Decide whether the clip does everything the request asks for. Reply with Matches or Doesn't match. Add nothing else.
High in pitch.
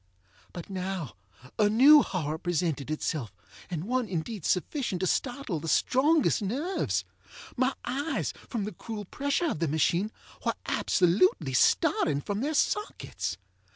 Matches